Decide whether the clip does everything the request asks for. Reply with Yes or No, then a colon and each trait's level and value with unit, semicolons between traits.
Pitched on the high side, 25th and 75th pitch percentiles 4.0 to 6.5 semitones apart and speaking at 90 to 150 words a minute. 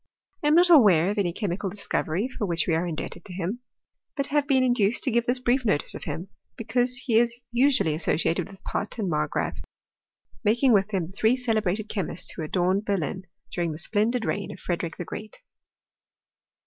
No: high, 205 Hz; wide, 5.5 semitones; average, 195 wpm